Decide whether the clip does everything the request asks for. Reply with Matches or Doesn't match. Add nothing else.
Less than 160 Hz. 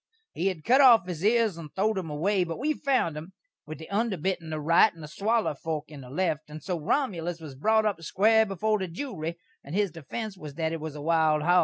Doesn't match